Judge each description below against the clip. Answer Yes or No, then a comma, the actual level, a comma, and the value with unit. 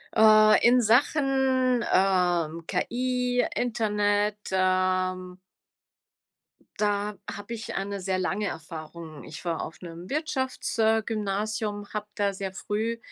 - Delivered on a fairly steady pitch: No, average, 3.7 semitones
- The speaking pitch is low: No, high, 205 Hz